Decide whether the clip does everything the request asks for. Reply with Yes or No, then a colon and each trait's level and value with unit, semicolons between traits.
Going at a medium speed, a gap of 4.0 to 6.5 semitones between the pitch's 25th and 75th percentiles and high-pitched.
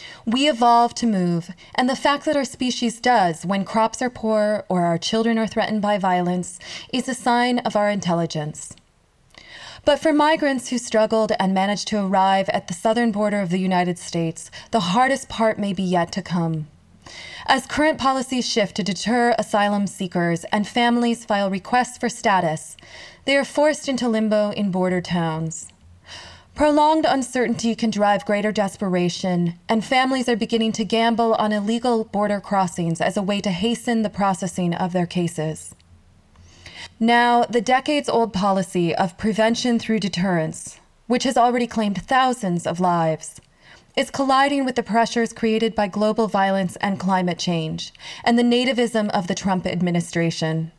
Yes: average, 160 wpm; average, 4.8 semitones; high, 210 Hz